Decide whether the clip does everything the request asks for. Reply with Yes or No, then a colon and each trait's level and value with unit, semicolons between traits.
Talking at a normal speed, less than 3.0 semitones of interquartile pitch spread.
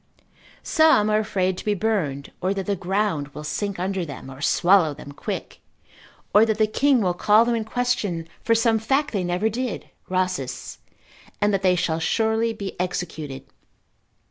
No: average, 175 wpm; average, 4.0 semitones